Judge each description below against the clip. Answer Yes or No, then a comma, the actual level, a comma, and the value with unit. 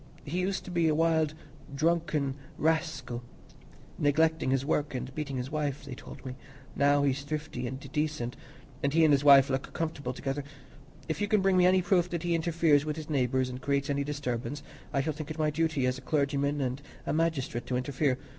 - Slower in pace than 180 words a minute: No, average, 200 wpm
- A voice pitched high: No, medium, 145 Hz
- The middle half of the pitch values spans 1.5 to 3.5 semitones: Yes, average, 3.0 semitones